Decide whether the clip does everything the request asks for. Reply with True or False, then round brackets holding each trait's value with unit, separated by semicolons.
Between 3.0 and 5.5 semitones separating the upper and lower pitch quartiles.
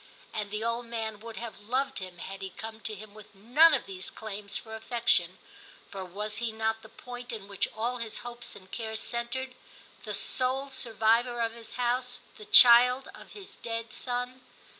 False (2.4 semitones)